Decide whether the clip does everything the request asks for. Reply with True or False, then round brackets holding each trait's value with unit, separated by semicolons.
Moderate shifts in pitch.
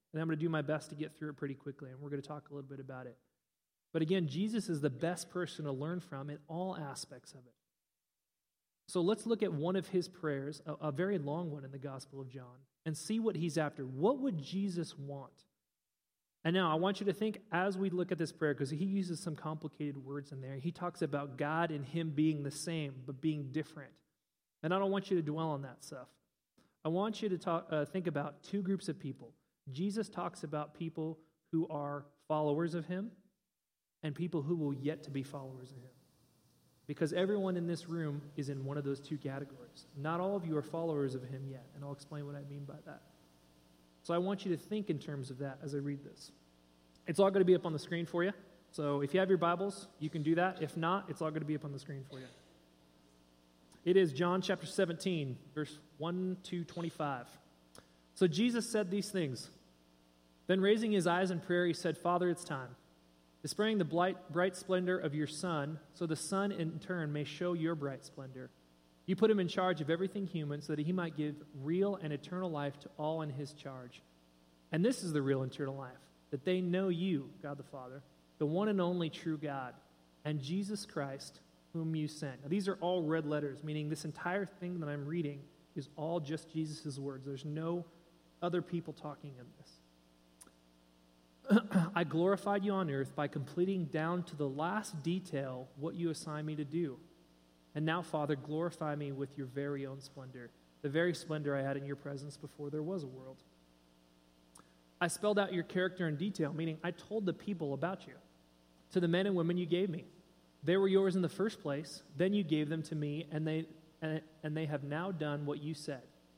True (4.0 semitones)